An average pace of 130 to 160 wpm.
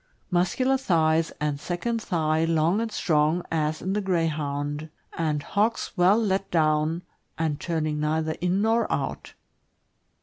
Yes: average, 140 wpm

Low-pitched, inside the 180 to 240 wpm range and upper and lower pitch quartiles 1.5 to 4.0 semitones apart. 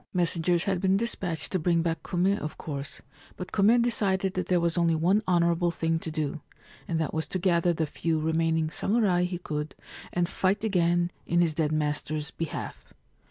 No: medium, 170 Hz; average, 185 wpm; narrow, 2.4 semitones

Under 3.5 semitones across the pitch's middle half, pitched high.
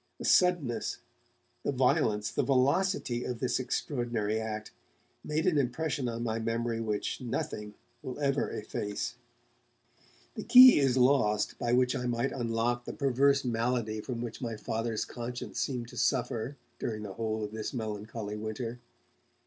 No: average, 3.0 semitones; low, 120 Hz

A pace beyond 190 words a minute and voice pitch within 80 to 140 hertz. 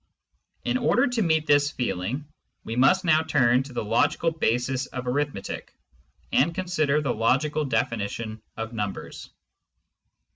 No: slow, 135 wpm; low, 135 Hz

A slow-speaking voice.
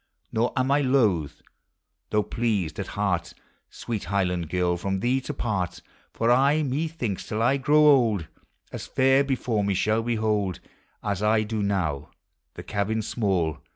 No: average, 155 wpm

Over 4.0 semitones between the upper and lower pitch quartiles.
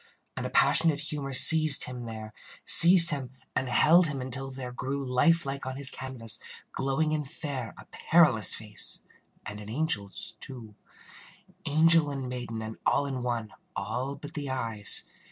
No: average, 3.7 semitones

